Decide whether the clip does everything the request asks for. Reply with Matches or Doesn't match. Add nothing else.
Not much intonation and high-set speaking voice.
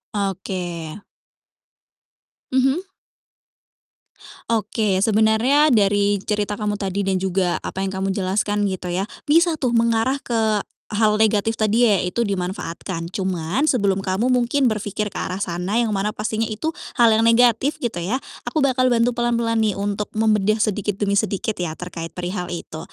Doesn't match